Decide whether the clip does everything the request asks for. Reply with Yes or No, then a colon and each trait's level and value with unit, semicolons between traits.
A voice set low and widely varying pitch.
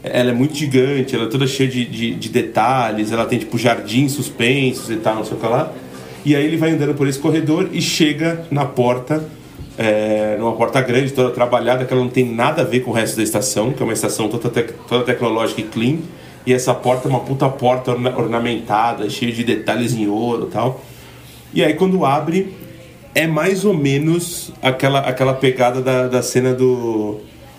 No: low, 125 Hz; average, 2.8 semitones